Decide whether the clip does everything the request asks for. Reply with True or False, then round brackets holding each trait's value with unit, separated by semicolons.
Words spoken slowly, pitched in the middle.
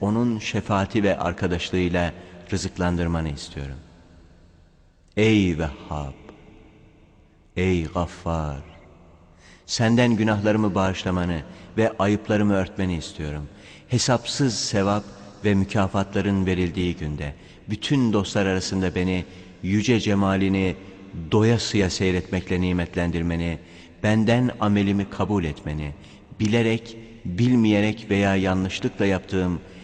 False (85 wpm; 95 Hz)